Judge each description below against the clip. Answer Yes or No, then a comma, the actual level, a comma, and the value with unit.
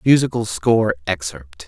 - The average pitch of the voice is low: Yes, very low, 95 Hz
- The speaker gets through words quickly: No, slow, 105 wpm